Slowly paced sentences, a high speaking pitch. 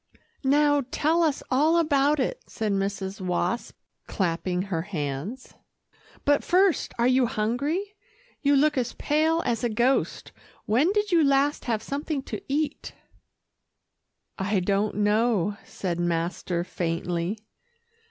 Yes: slow, 125 wpm; high, 235 Hz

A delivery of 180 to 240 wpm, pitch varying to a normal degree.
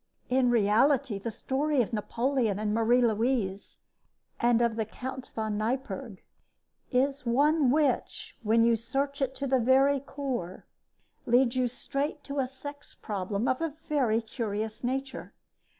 No: average, 145 wpm; average, 3.4 semitones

